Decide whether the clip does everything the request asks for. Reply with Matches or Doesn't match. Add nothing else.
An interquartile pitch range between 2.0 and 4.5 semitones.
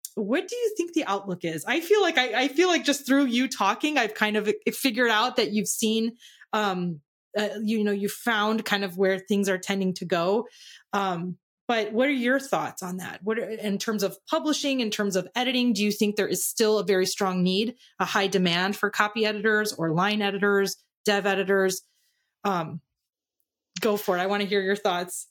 Matches